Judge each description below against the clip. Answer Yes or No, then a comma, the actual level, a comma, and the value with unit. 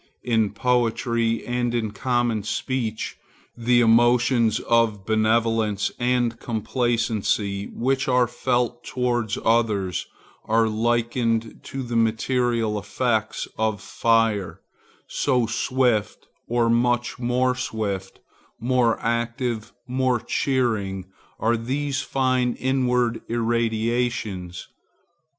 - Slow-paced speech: Yes, slow, 95 wpm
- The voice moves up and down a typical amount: No, narrow, 1.9 semitones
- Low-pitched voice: Yes, low, 115 Hz